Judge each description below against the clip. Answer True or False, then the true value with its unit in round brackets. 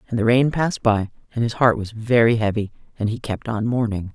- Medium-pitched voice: False (115 Hz)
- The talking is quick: True (230 wpm)